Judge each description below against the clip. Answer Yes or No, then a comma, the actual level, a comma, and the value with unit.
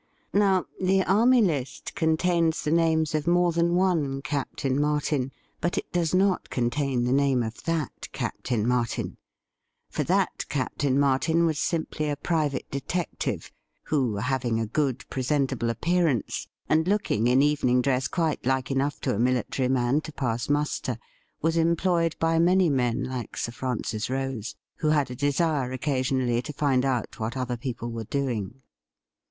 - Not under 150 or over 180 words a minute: Yes, average, 155 wpm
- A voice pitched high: No, medium, 140 Hz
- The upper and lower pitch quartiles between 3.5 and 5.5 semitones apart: Yes, average, 4.4 semitones